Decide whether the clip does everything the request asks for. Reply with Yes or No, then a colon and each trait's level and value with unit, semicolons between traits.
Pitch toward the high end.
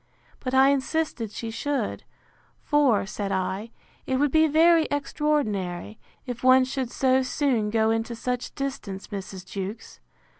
Yes: very high, 255 Hz